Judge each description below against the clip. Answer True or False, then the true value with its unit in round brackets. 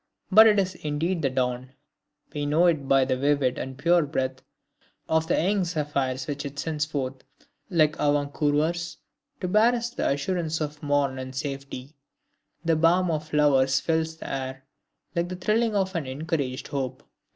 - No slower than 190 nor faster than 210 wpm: False (170 wpm)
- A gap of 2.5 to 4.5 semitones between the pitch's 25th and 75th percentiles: True (3.8 semitones)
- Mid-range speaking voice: True (150 Hz)